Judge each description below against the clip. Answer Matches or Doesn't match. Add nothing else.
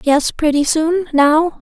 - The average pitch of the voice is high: Matches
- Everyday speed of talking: Matches